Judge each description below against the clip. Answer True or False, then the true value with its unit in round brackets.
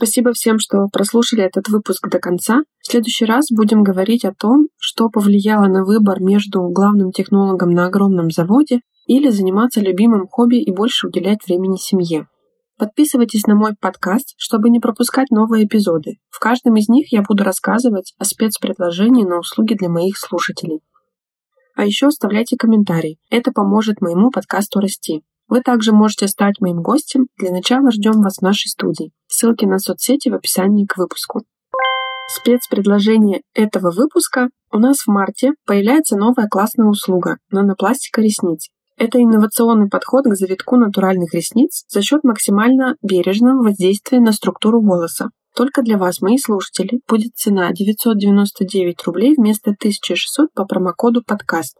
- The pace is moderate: True (150 wpm)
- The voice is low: False (215 Hz)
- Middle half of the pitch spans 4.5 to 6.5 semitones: False (4.0 semitones)